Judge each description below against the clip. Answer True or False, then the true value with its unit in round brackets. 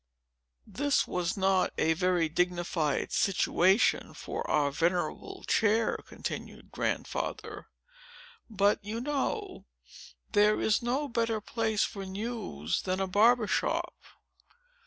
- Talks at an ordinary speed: False (110 wpm)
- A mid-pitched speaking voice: False (200 Hz)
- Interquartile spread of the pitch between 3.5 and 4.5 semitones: True (4.2 semitones)